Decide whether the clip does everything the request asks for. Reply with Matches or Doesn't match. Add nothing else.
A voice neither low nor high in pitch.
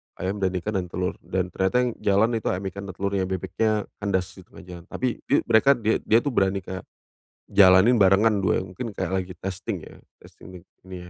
Doesn't match